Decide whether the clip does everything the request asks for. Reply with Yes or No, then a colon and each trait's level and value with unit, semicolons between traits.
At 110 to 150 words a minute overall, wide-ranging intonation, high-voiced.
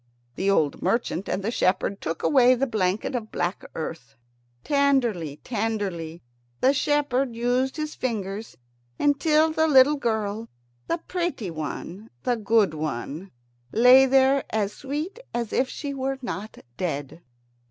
Yes: slow, 135 wpm; wide, 6.0 semitones; high, 230 Hz